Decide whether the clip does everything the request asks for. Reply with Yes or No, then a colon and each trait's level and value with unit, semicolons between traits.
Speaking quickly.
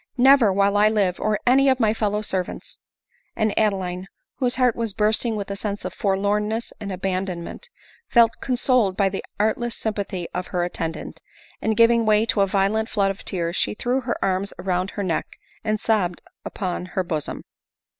No: average, 185 wpm